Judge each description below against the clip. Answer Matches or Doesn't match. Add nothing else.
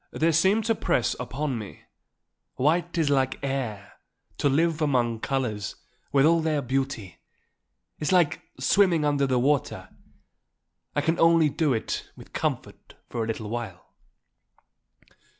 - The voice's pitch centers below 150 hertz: Matches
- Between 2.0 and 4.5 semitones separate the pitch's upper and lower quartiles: Doesn't match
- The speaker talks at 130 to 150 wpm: Matches